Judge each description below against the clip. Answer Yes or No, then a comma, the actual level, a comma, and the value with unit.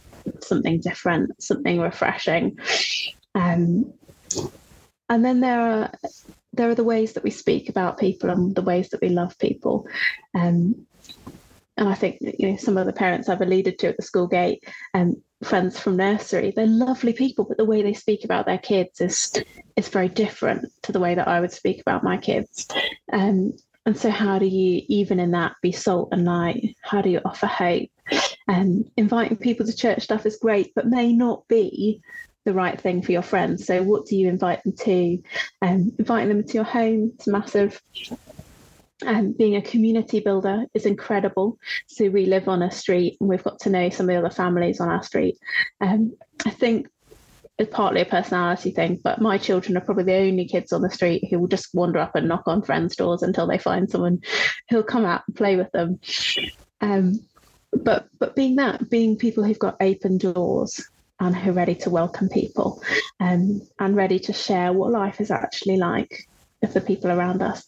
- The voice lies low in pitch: No, high, 200 Hz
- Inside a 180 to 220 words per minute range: Yes, average, 200 wpm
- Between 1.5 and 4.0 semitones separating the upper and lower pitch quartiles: Yes, average, 3.3 semitones